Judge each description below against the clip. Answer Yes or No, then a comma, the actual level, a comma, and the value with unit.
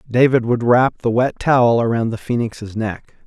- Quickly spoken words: No, average, 185 wpm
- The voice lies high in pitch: No, low, 120 Hz